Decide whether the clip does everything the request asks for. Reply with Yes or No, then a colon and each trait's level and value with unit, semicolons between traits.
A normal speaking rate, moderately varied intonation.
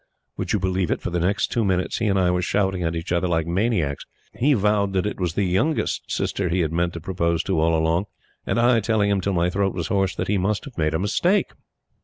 No: fast, 255 wpm; average, 3.1 semitones